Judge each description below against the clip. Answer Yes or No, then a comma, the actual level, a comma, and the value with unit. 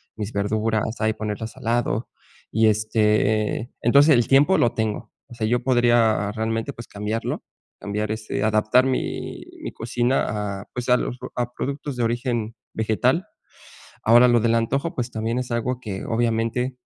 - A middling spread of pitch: No, narrow, 2.1 semitones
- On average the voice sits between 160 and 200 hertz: No, low, 115 Hz